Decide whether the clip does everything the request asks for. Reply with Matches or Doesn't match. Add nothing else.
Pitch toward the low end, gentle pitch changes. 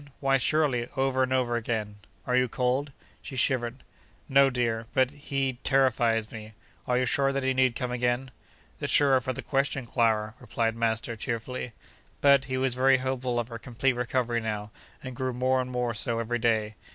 Matches